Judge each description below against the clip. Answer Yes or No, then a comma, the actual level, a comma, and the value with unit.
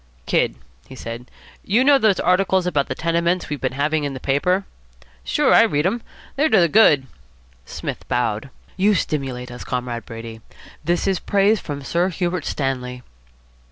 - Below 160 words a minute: No, average, 165 wpm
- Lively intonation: Yes, wide, 6.6 semitones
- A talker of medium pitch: Yes, medium, 155 Hz